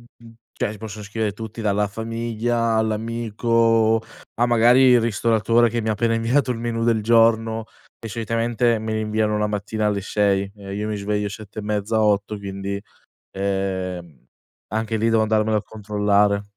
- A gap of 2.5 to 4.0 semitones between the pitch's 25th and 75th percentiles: No, narrow, 1.8 semitones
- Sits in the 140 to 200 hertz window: No, low, 110 Hz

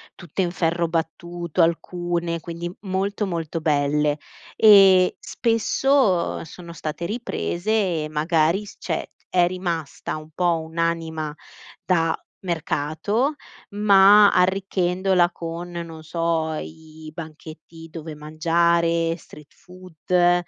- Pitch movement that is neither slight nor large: No, narrow, 2.3 semitones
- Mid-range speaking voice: Yes, medium, 170 Hz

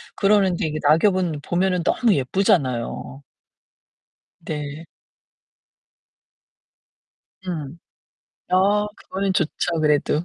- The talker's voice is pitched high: No, medium, 170 Hz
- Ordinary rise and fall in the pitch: Yes, average, 4.2 semitones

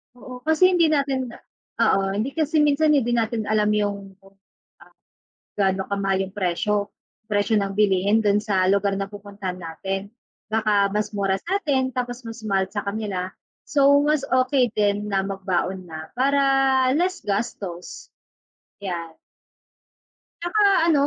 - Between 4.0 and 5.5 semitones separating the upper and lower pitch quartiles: Yes, average, 5.2 semitones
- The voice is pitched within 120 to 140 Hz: No, high, 210 Hz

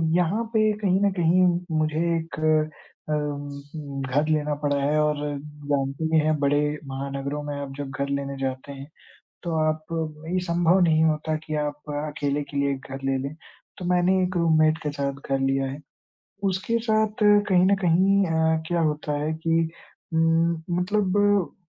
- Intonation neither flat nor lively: Yes, average, 3.5 semitones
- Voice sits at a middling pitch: Yes, medium, 155 Hz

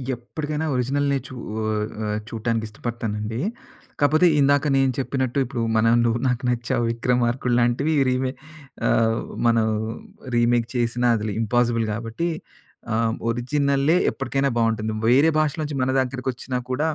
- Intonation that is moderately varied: Yes, average, 3.1 semitones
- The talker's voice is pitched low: Yes, low, 120 Hz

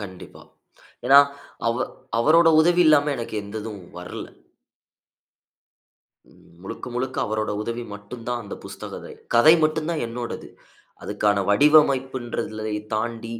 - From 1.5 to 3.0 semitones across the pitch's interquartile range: No, average, 4.7 semitones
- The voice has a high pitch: No, low, 120 Hz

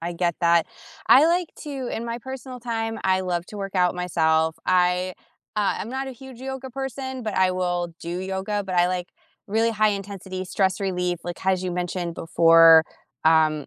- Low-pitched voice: No, medium, 185 Hz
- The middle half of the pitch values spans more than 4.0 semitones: Yes, average, 4.6 semitones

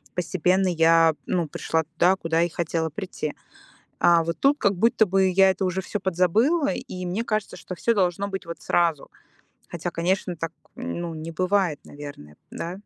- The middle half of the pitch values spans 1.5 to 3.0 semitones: Yes, average, 2.7 semitones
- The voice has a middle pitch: Yes, medium, 180 Hz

